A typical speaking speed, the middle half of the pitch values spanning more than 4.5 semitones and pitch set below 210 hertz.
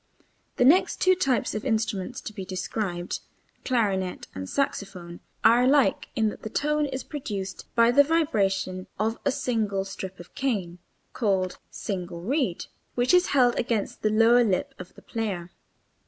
No: average, 155 wpm; average, 5.1 semitones; high, 215 Hz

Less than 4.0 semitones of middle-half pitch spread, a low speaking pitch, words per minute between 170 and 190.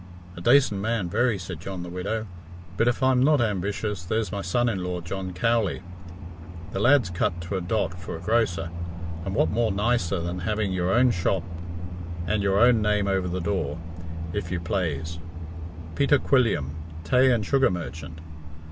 No: average, 4.5 semitones; very low, 95 Hz; average, 175 wpm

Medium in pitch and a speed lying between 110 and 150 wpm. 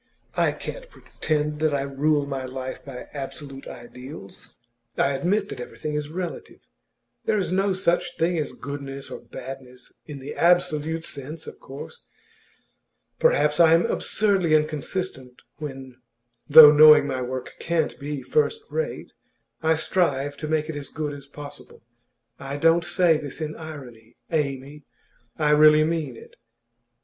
Yes: medium, 150 Hz; average, 145 wpm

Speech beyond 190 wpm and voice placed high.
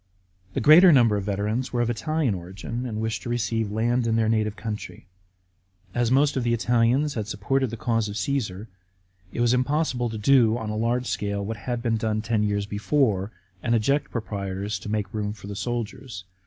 No: average, 200 wpm; low, 115 Hz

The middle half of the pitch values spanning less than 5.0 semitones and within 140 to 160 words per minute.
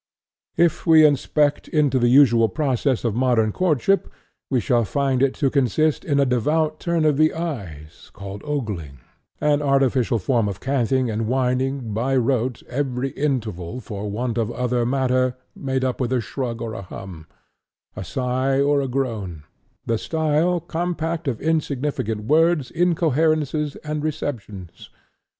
Yes: average, 4.4 semitones; average, 150 wpm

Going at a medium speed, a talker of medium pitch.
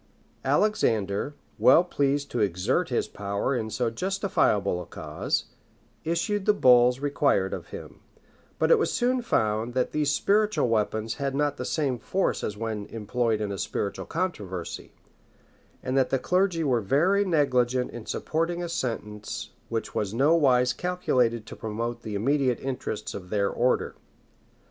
No: average, 155 wpm; low, 125 Hz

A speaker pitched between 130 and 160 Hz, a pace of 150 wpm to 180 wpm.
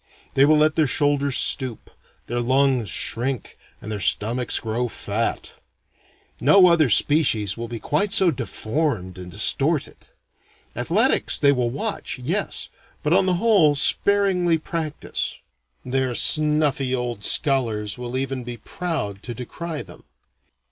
No: low, 135 Hz; slow, 135 wpm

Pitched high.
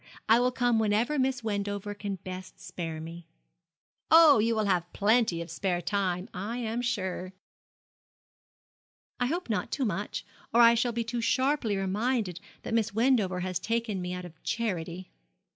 Yes: high, 210 Hz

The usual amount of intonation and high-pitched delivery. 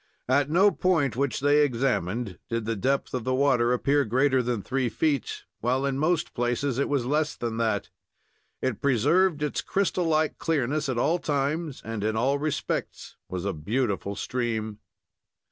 No: average, 3.7 semitones; low, 130 Hz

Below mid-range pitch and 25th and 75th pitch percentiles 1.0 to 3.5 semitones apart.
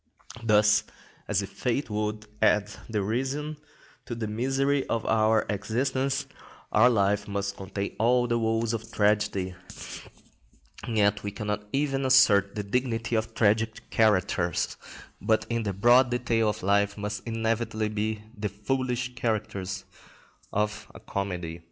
Yes: low, 110 Hz; narrow, 2.5 semitones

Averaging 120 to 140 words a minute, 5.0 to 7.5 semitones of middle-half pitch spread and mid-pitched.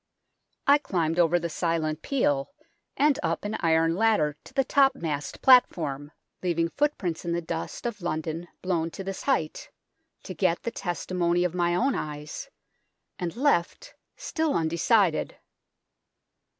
Yes: slow, 135 wpm; wide, 5.6 semitones; medium, 175 Hz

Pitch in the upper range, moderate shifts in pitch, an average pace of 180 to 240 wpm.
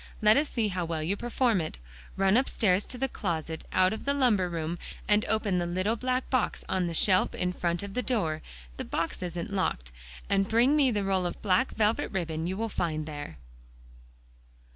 Yes: high, 195 Hz; average, 4.6 semitones; average, 200 wpm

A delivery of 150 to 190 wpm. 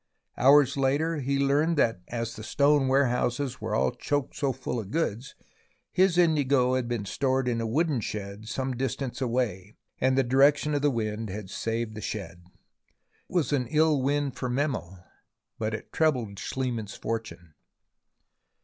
Yes: average, 160 wpm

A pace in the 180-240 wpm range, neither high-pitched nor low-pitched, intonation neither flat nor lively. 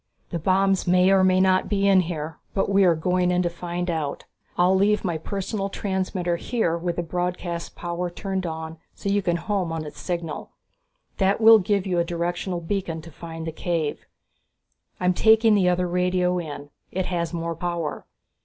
No: average, 190 wpm; medium, 180 Hz; narrow, 2.1 semitones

